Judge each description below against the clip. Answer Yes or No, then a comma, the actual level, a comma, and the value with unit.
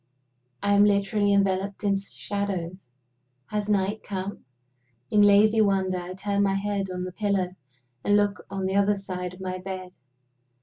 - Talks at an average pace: Yes, average, 160 wpm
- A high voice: Yes, high, 195 Hz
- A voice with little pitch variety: Yes, narrow, 1.4 semitones